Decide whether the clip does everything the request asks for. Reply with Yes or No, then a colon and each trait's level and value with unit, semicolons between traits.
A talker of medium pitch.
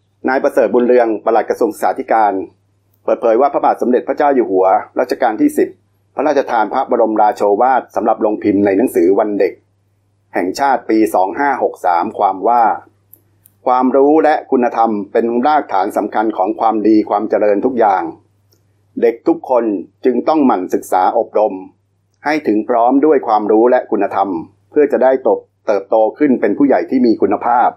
No: low, 110 Hz